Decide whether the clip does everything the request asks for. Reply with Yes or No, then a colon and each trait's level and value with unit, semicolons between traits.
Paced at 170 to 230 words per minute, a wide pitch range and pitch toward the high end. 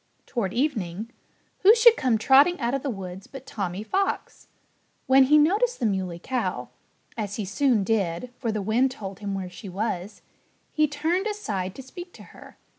Yes: average, 180 wpm; wide, 6.8 semitones; high, 235 Hz